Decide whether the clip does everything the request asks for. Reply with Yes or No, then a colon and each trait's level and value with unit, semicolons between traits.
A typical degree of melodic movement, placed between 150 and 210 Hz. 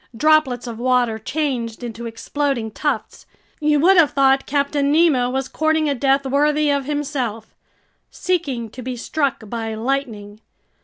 No: average, 3.9 semitones; very high, 270 Hz